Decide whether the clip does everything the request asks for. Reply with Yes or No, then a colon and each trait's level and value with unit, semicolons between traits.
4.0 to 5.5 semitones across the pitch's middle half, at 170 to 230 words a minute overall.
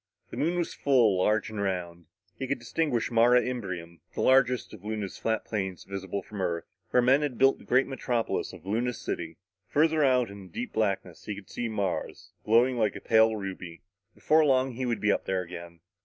Yes: average, 4.9 semitones; average, 200 wpm